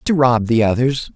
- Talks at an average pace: No, fast, 210 wpm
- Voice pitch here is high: No, low, 125 Hz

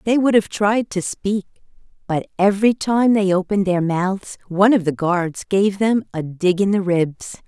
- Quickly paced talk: No, average, 195 wpm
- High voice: Yes, high, 195 Hz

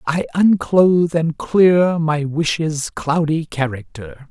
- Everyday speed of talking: No, slow, 110 wpm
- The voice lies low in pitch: No, medium, 160 Hz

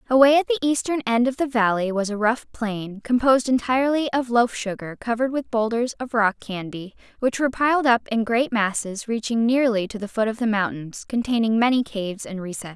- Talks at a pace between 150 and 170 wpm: No, average, 200 wpm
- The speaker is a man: No, female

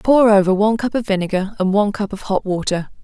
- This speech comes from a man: No, female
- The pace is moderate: No, fast, 235 wpm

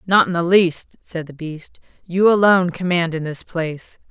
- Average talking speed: Yes, average, 190 wpm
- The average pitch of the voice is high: No, medium, 175 Hz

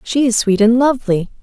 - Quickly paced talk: Yes, fast, 210 wpm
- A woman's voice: Yes, female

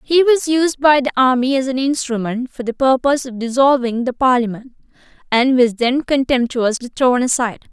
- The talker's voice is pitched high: Yes, very high, 255 Hz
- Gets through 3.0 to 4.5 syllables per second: No, 5.2 syllables/s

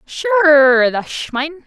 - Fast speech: No, slow, 110 wpm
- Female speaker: Yes, female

